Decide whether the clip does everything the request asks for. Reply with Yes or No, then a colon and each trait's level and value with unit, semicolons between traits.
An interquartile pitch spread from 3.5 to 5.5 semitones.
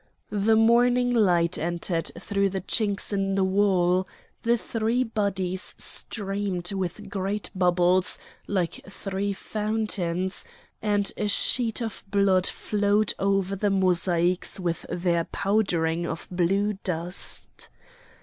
No: narrow, 2.5 semitones